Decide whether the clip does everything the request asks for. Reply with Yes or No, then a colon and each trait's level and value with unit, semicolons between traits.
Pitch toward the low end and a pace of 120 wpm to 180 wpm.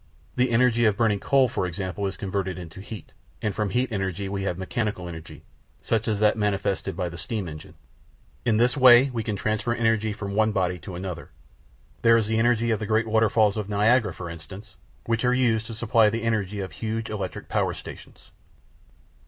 No: low, 105 Hz; average, 195 wpm